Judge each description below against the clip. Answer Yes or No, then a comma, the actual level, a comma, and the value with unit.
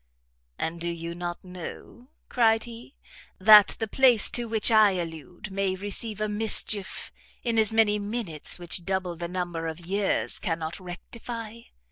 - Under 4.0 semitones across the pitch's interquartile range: No, average, 4.3 semitones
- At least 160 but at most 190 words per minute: No, average, 150 wpm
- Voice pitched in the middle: No, high, 195 Hz